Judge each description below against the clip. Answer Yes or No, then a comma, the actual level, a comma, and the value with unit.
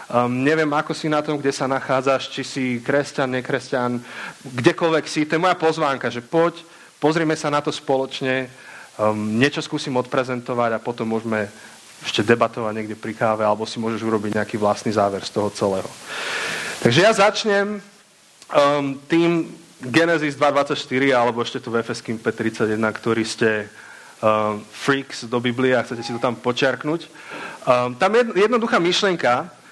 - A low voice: Yes, low, 130 Hz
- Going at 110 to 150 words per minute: No, average, 160 wpm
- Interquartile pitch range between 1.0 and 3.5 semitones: No, average, 4.9 semitones